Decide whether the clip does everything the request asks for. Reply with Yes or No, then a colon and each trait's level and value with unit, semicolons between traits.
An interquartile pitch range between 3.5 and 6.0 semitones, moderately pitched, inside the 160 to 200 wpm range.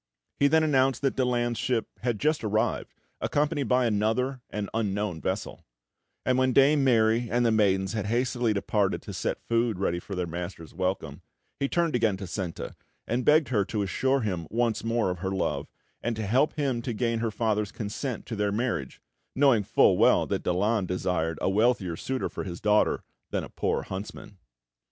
No: average, 4.3 semitones; low, 110 Hz; average, 185 wpm